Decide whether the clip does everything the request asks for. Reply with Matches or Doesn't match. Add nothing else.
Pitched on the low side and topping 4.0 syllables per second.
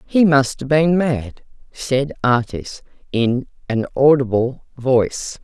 Doesn't match